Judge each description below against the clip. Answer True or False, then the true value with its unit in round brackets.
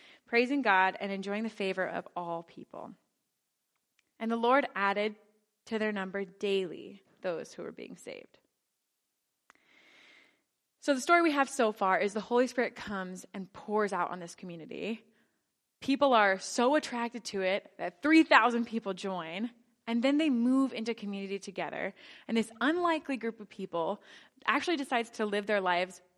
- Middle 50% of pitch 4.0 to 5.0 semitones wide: True (4.4 semitones)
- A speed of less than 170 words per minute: True (160 wpm)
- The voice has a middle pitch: False (215 Hz)